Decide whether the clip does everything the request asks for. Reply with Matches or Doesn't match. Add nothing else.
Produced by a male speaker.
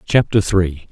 Matches